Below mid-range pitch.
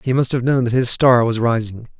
Yes: low, 120 Hz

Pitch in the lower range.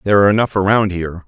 Yes: low, 100 Hz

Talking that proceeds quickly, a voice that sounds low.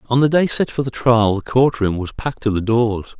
Yes: fast, 280 wpm; low, 120 Hz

